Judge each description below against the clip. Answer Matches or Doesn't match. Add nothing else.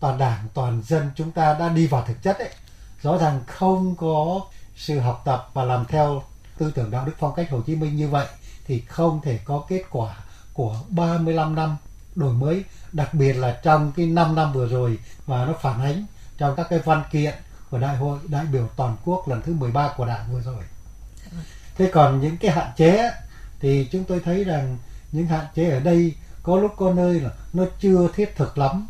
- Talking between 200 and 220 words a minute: Matches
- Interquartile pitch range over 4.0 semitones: Matches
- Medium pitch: Matches